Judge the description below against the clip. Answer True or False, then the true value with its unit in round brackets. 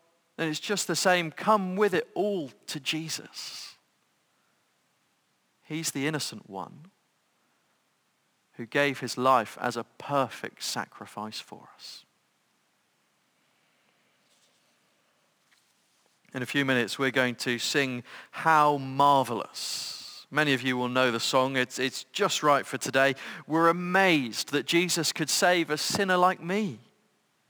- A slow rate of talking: True (125 wpm)